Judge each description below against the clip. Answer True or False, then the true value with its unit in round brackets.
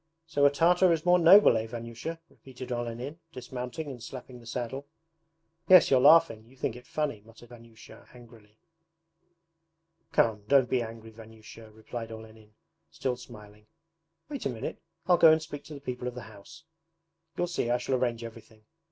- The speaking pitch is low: True (125 Hz)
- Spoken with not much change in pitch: False (4.1 semitones)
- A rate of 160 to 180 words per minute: True (170 wpm)